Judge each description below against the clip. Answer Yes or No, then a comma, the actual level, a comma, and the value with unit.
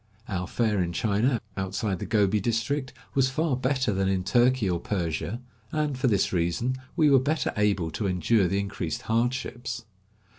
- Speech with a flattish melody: No, average, 5.2 semitones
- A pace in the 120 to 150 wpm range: No, average, 165 wpm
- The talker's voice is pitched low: Yes, low, 110 Hz